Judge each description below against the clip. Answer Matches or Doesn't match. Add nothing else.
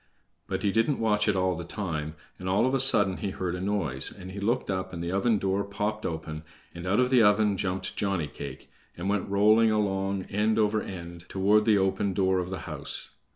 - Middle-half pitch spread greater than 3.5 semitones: Doesn't match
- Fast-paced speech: Matches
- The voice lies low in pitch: Matches